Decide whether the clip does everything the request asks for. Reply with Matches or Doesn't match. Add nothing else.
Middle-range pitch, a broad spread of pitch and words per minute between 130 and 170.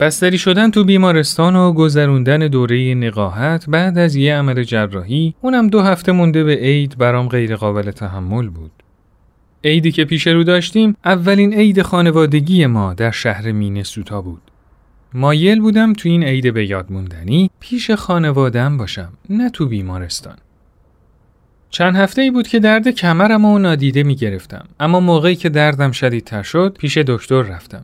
Matches